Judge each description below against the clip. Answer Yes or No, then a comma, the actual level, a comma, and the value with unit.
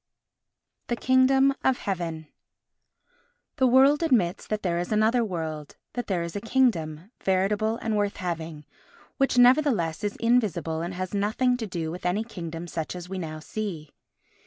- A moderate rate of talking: Yes, average, 160 wpm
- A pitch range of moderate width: No, wide, 6.0 semitones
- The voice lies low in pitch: No, high, 200 Hz